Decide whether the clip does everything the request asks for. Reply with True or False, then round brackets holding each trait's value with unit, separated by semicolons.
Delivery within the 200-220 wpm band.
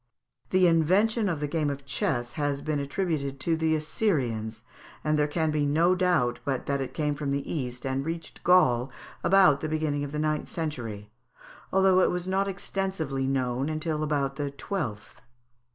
False (175 wpm)